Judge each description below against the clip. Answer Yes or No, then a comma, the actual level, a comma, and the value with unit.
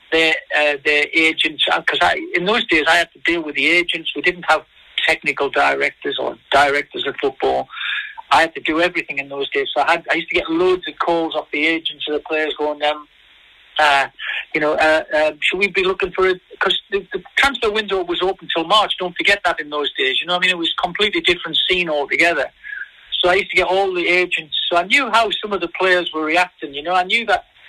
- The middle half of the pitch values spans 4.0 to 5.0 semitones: Yes, average, 4.3 semitones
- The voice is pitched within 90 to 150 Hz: No, medium, 175 Hz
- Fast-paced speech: Yes, fast, 245 wpm